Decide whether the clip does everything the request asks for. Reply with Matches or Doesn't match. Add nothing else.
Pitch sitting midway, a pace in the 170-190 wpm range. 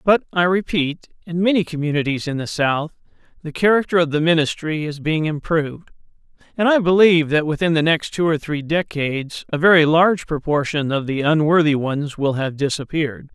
Matches